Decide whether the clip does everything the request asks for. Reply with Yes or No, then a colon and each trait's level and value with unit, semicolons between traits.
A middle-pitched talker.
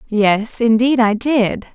No: high, 230 Hz